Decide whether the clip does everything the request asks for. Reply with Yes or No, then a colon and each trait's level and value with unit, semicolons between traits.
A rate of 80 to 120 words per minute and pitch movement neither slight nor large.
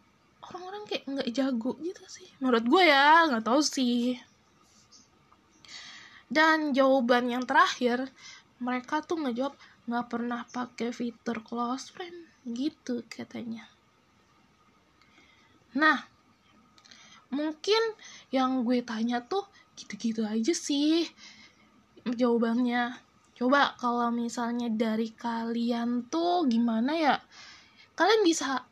Yes: average, 100 wpm; average, 4.4 semitones